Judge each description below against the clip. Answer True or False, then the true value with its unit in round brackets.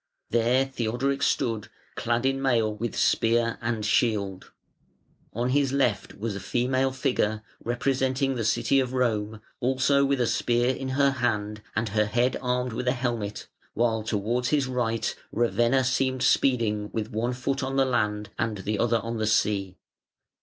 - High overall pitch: False (120 Hz)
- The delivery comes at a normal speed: True (160 wpm)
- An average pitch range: True (3.0 semitones)